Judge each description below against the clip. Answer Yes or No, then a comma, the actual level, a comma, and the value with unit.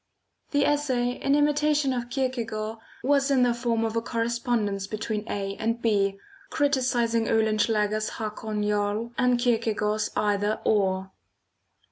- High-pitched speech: Yes, high, 230 Hz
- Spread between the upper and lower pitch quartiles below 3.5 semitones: Yes, average, 2.9 semitones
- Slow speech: Yes, slow, 125 wpm